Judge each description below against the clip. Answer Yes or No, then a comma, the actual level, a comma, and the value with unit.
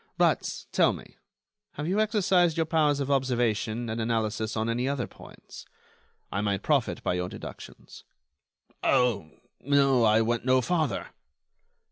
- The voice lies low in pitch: Yes, low, 125 Hz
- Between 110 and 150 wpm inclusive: Yes, average, 140 wpm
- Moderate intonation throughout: Yes, average, 4.6 semitones